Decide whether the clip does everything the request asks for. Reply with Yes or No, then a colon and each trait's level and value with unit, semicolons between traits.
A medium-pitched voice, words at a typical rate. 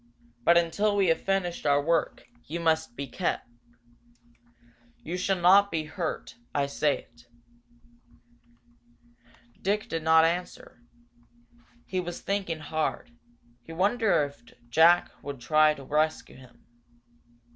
No: medium, 165 Hz; slow, 125 wpm